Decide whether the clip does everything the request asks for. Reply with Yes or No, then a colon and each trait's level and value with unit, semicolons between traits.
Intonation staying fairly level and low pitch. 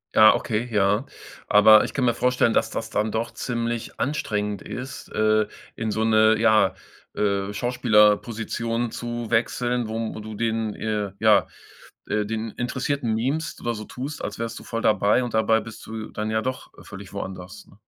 Yes: narrow, 1.9 semitones; low, 110 Hz